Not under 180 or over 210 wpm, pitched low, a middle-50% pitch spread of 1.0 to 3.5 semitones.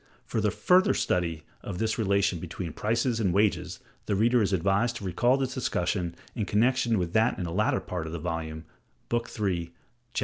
No: average, 195 wpm; low, 100 Hz; average, 5.1 semitones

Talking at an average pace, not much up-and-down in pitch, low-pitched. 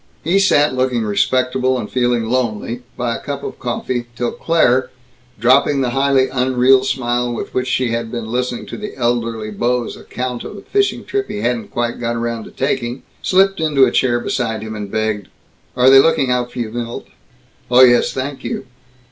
Yes: average, 190 wpm; narrow, 1.9 semitones; low, 125 Hz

